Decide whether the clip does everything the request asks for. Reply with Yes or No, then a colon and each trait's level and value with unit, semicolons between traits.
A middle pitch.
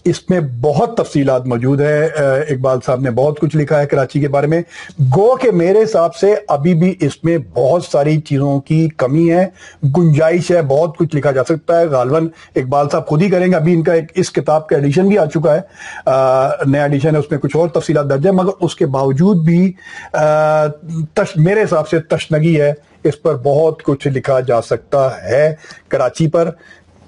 Yes: medium, 155 Hz